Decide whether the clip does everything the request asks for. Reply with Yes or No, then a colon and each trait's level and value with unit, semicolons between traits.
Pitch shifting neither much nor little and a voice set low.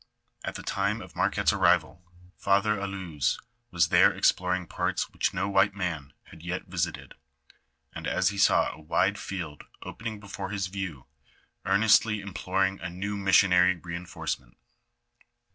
No: narrow, 2.2 semitones; very low, 95 Hz